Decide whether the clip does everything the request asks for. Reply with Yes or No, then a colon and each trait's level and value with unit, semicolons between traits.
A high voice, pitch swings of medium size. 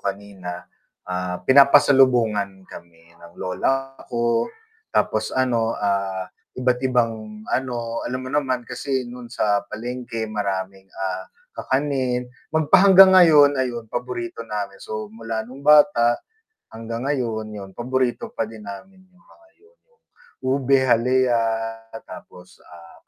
No: low, 120 Hz; average, 4.2 semitones